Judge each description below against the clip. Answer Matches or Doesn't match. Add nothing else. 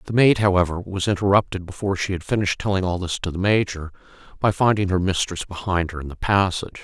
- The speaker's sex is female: Doesn't match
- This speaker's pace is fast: Matches